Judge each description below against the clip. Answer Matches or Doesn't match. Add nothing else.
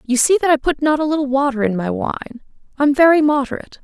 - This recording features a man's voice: Doesn't match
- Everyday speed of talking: Doesn't match